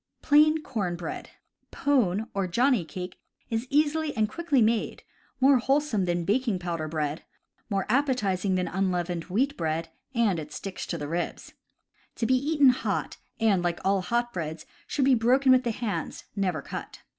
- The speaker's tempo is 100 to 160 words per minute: No, average, 170 wpm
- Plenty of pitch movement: Yes, wide, 6.6 semitones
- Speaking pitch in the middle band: No, high, 210 Hz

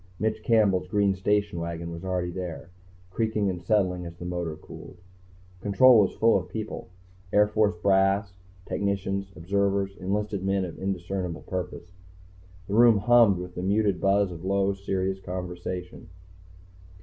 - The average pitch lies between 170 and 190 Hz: No, very low, 95 Hz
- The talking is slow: No, average, 145 wpm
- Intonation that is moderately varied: No, narrow, 2.2 semitones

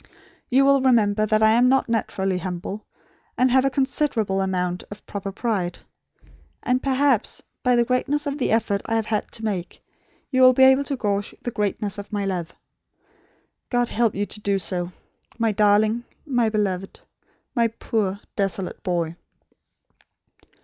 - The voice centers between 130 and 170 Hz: No, high, 215 Hz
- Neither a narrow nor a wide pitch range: Yes, average, 4.2 semitones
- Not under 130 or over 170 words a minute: Yes, average, 160 wpm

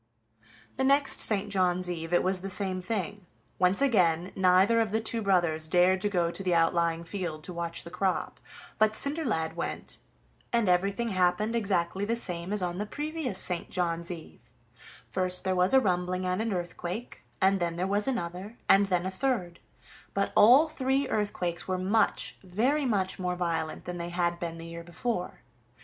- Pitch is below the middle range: No, medium, 185 Hz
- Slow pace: No, average, 180 wpm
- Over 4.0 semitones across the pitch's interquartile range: No, average, 3.3 semitones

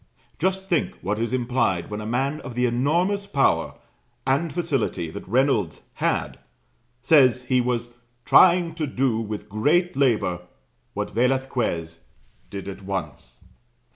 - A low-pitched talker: Yes, low, 125 Hz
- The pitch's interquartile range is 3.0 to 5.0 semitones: No, wide, 5.5 semitones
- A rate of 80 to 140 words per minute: Yes, slow, 135 wpm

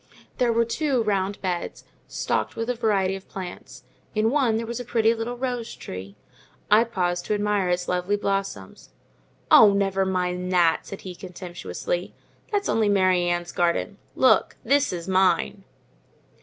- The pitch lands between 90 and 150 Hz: No, high, 195 Hz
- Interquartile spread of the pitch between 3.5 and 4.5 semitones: Yes, average, 4.1 semitones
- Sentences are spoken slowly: No, average, 155 wpm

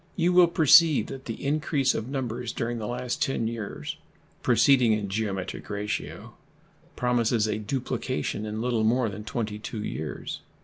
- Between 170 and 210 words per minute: No, average, 145 wpm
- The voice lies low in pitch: Yes, low, 115 Hz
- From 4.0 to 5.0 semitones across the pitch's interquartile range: No, average, 3.6 semitones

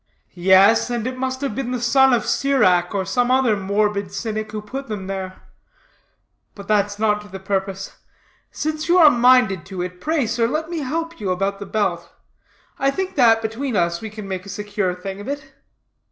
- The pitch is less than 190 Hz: No, high, 215 Hz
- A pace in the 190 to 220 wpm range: Yes, average, 195 wpm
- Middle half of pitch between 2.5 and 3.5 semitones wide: No, average, 5.0 semitones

